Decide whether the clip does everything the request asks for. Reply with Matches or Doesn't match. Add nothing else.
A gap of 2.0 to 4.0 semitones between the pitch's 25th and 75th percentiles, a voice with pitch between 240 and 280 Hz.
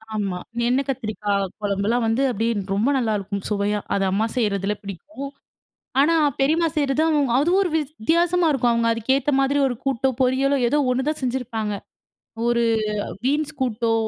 Doesn't match